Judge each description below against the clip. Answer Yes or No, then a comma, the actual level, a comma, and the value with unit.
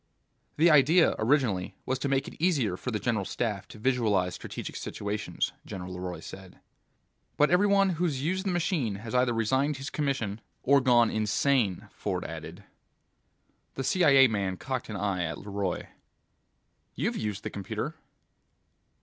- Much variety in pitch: Yes, wide, 5.7 semitones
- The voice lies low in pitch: Yes, low, 120 Hz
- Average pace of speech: Yes, average, 150 wpm